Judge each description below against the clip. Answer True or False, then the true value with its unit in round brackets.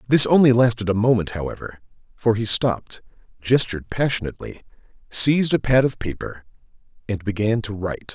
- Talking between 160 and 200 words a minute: False (145 wpm)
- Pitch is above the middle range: False (115 Hz)